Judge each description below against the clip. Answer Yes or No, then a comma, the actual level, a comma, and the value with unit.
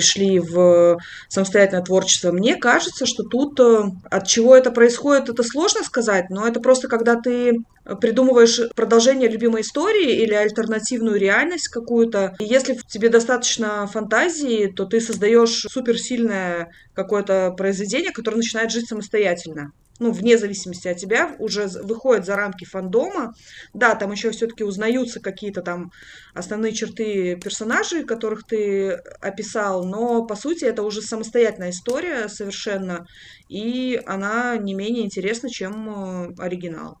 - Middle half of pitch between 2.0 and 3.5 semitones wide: Yes, average, 3.2 semitones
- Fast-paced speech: No, average, 130 wpm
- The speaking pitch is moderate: No, high, 220 Hz